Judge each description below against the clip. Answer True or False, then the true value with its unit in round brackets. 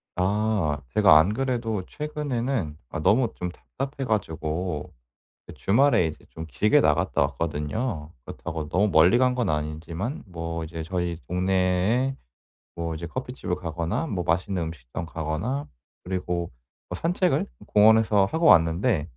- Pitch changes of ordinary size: False (5.7 semitones)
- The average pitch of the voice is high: False (90 Hz)